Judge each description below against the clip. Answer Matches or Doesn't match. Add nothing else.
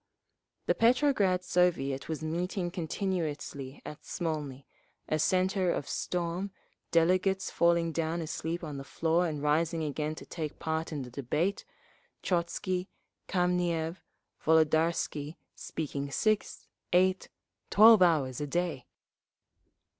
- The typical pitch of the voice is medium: Matches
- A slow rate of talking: Matches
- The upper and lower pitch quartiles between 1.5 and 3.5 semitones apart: Matches